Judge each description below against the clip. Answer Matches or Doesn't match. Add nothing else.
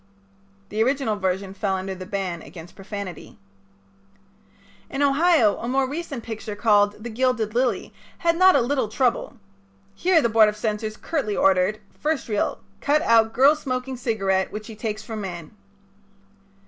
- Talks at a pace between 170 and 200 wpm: Doesn't match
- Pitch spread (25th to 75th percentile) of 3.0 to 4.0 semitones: Doesn't match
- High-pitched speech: Matches